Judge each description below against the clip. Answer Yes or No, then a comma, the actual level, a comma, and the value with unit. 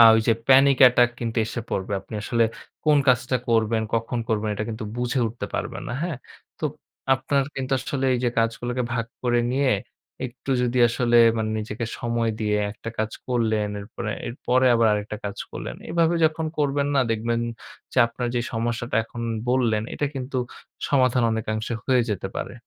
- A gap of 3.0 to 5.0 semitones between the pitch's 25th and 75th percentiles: No, narrow, 2.6 semitones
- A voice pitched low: Yes, low, 120 Hz